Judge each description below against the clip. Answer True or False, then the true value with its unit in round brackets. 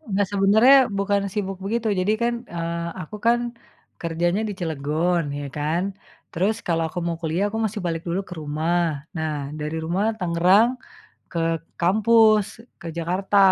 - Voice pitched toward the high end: False (180 Hz)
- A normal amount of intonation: True (3.7 semitones)